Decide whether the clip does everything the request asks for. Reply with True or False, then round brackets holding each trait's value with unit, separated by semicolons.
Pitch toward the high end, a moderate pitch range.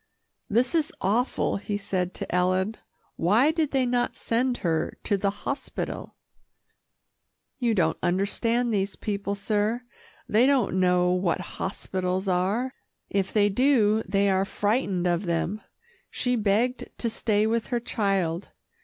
True (205 Hz; 4.2 semitones)